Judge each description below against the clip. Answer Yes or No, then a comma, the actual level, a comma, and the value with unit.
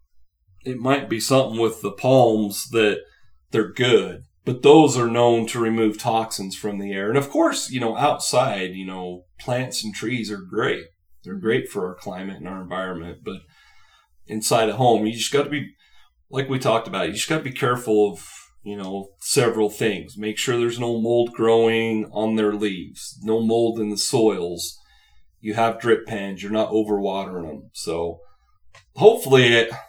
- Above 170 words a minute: Yes, average, 180 wpm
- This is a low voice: Yes, low, 110 Hz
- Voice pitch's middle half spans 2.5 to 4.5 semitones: Yes, average, 3.5 semitones